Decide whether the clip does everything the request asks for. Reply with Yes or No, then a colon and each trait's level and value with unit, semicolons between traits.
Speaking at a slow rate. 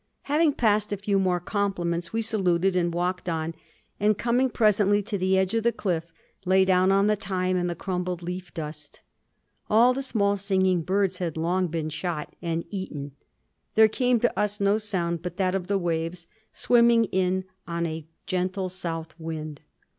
No: average, 175 wpm